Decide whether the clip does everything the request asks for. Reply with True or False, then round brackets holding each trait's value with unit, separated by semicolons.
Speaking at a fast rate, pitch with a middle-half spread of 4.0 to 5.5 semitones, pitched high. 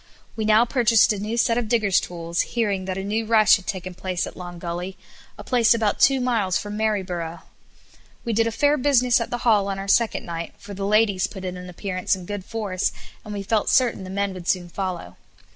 False (225 wpm; 3.5 semitones; 200 Hz)